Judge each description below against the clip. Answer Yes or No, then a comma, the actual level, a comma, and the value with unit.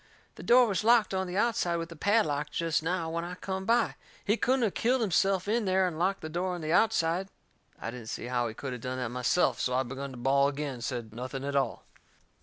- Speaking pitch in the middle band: Yes, medium, 165 Hz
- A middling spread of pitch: No, wide, 6.3 semitones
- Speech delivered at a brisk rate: Yes, fast, 245 wpm